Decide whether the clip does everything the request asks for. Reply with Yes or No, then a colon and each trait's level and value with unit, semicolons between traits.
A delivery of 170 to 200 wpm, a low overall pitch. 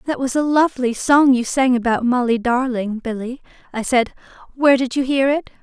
No: average, 190 wpm; very high, 255 Hz